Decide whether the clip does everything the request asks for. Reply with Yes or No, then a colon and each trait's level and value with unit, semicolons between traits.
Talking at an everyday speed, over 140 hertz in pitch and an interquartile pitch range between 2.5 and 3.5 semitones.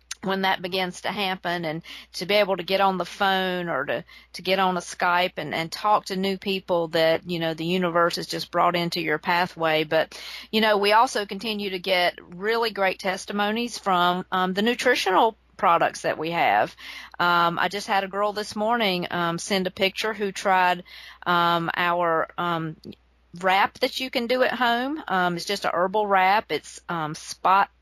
Yes: average, 195 wpm; medium, 185 Hz; average, 2.8 semitones